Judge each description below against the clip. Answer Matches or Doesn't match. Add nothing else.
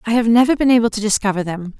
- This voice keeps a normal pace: Doesn't match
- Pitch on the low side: Doesn't match